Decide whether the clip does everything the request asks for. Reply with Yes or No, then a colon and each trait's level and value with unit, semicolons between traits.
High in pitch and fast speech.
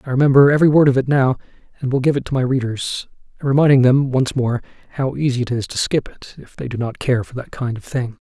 No: low, 130 Hz; fast, 255 wpm